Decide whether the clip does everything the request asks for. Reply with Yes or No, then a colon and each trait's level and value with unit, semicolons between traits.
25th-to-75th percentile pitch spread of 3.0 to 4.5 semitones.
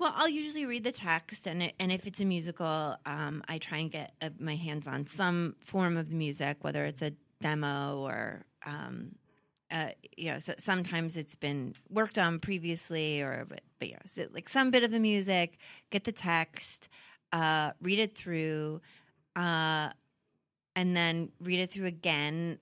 Yes: average, 3.6 semitones